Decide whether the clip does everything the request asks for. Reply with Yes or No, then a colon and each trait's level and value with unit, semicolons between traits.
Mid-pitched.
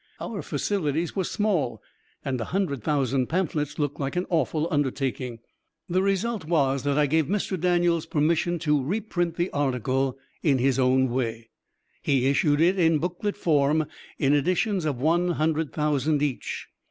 Yes: medium, 150 Hz